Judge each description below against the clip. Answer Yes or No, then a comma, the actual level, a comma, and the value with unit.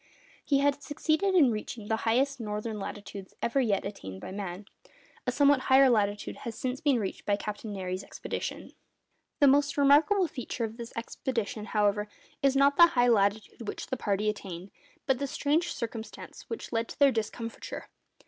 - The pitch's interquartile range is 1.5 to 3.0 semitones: No, average, 5.0 semitones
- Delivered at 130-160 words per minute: No, average, 170 wpm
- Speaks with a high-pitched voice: Yes, high, 230 Hz